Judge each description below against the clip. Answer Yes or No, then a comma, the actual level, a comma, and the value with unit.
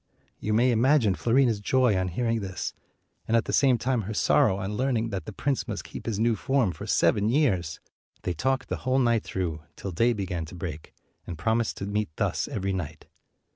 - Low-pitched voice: Yes, low, 110 Hz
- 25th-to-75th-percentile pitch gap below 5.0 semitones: Yes, average, 4.6 semitones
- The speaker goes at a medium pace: No, fast, 210 wpm